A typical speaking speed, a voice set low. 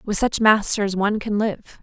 No: average, 195 wpm; high, 210 Hz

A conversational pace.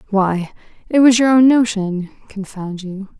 Yes: average, 150 wpm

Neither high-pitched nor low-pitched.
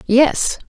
No: very high, 265 Hz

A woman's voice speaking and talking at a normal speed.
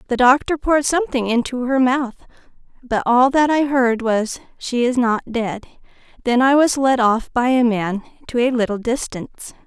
Yes: female; average, 180 wpm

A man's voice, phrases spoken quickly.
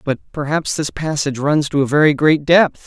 Yes: male; fast, 210 wpm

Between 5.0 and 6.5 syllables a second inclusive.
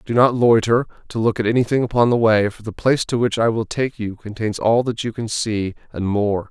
Yes: 5.5 syllables/s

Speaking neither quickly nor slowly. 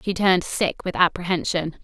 Yes: average, 165 wpm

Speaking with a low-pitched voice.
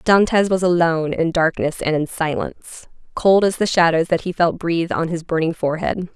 No: medium, 170 Hz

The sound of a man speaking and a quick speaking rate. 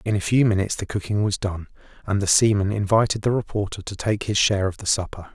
Yes: male; fast, 235 wpm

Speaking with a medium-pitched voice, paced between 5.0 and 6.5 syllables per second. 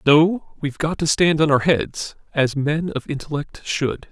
No: medium, 150 Hz; 4.2 syllables/s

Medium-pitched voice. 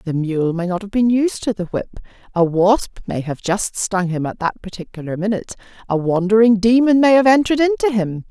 No: high, 205 Hz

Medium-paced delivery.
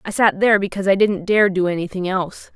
No: fast, 235 wpm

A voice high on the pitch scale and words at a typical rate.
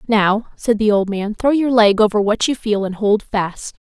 No: high, 215 Hz; fast, 230 wpm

